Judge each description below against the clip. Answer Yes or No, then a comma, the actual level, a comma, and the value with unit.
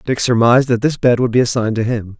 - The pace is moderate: No, fast, 275 wpm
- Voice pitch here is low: Yes, low, 120 Hz